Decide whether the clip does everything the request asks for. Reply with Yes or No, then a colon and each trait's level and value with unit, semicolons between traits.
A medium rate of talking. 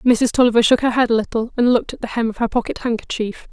No: fast, 275 wpm